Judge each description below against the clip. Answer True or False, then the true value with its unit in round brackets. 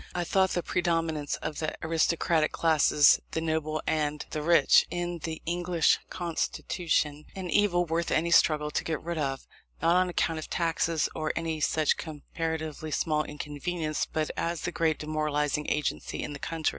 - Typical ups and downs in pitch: False (1.8 semitones)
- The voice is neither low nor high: True (160 Hz)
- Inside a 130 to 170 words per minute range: True (165 wpm)